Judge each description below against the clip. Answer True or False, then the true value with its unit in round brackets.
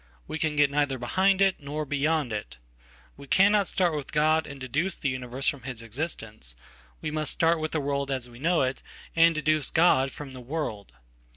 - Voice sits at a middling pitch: True (145 Hz)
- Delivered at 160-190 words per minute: True (180 wpm)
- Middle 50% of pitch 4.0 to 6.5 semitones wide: False (3.6 semitones)